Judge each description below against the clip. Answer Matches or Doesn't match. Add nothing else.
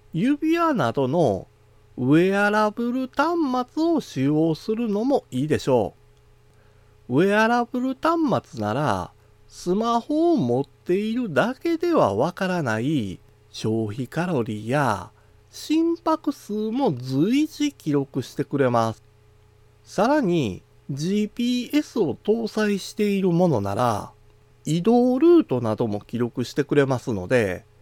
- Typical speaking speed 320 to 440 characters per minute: Doesn't match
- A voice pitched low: Doesn't match